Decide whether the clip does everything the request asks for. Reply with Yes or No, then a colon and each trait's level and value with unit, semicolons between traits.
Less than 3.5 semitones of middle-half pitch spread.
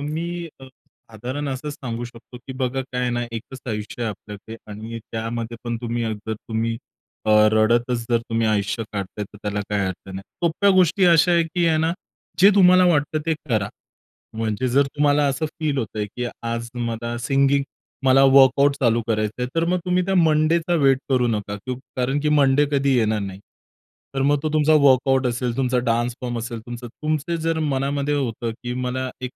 No: average, 4.1 semitones